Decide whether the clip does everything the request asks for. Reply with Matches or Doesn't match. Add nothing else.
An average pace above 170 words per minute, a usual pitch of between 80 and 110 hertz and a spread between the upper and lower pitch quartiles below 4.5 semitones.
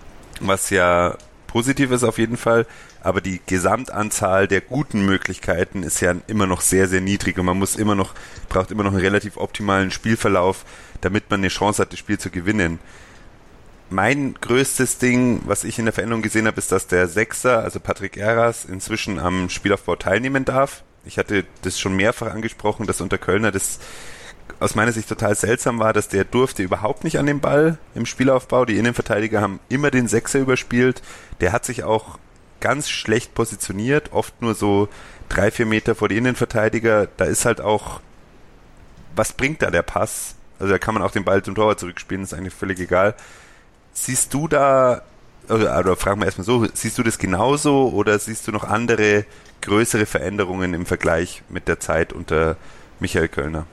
Matches